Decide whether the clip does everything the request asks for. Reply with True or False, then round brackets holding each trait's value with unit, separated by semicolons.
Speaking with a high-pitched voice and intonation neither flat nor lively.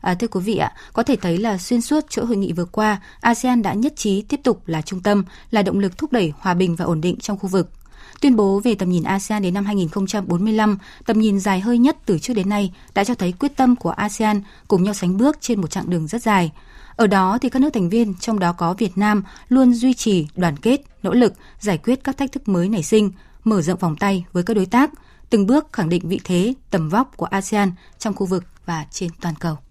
True (205 Hz; 4.1 semitones)